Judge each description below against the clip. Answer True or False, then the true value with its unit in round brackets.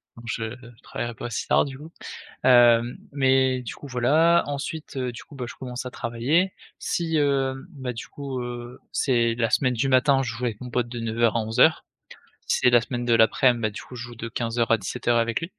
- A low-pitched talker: True (125 Hz)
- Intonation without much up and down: True (2.3 semitones)